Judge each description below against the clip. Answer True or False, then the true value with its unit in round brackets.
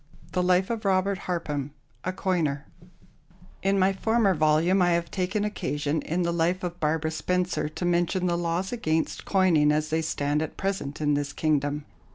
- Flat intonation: False (3.4 semitones)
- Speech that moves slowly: False (175 wpm)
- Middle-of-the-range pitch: True (170 Hz)